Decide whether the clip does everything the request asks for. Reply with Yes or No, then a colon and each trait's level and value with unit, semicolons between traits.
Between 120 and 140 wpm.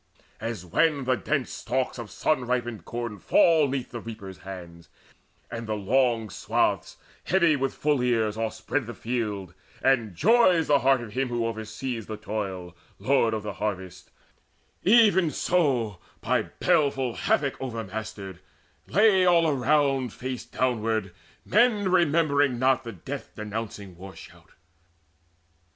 Yes: slow, 135 wpm